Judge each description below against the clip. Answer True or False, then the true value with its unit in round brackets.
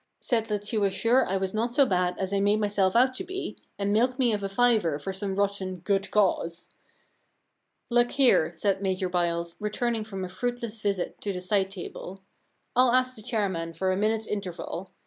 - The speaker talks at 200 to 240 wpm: True (205 wpm)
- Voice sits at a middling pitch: False (200 Hz)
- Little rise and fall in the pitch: False (3.4 semitones)